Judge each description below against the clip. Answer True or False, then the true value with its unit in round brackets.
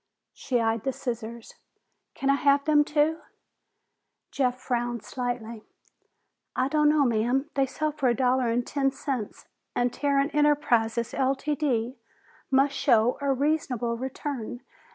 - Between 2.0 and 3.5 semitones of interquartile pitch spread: True (3.0 semitones)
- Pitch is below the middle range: False (260 Hz)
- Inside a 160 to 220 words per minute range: False (135 wpm)